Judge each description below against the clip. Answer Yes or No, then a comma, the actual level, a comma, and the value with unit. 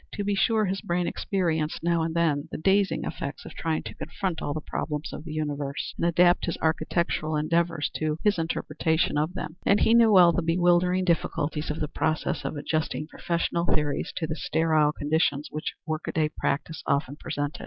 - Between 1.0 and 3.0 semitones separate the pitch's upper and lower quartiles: Yes, narrow, 2.5 semitones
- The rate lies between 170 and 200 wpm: Yes, average, 185 wpm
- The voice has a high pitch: No, medium, 160 Hz